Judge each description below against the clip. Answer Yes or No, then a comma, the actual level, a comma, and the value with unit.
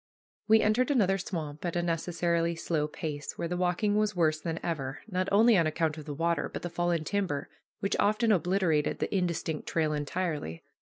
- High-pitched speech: No, medium, 170 Hz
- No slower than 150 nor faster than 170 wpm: No, average, 185 wpm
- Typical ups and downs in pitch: Yes, average, 3.6 semitones